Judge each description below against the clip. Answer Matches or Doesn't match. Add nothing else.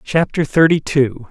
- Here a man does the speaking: Matches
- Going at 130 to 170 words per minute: Matches